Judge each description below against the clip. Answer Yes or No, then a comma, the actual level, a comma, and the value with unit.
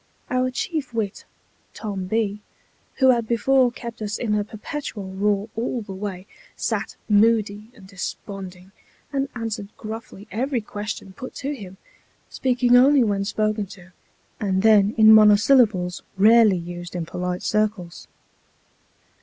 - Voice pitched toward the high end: Yes, high, 210 Hz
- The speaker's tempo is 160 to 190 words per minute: No, slow, 135 wpm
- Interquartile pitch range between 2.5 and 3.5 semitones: Yes, average, 3.1 semitones